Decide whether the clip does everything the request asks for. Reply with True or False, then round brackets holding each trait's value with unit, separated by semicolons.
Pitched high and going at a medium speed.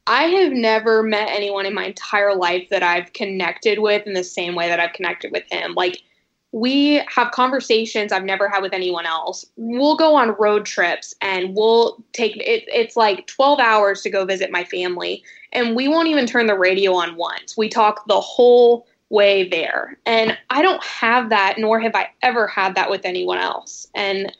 True (215 Hz; 195 wpm)